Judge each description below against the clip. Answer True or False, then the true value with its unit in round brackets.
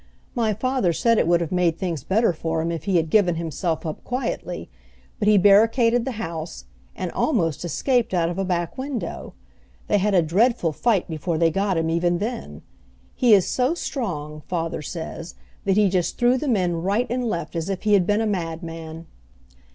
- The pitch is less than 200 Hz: True (185 Hz)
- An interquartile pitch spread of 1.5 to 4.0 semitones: False (5.2 semitones)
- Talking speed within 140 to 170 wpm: False (195 wpm)